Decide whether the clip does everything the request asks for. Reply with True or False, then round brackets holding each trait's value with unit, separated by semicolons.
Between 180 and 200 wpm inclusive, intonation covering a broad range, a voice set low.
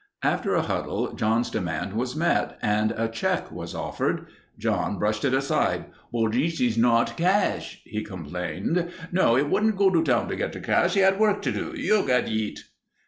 True (185 wpm; 8.2 semitones; 125 Hz)